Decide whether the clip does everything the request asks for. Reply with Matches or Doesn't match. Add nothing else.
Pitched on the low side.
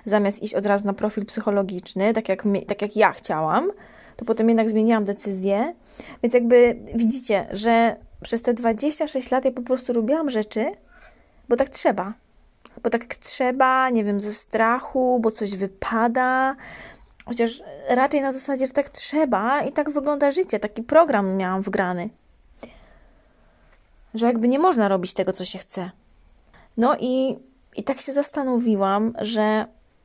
Doesn't match